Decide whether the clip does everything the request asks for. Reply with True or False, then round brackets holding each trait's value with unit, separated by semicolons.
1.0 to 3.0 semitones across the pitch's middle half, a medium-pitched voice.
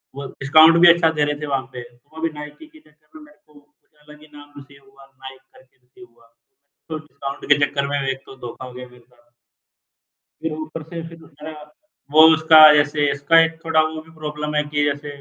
True (2.5 semitones; 145 Hz)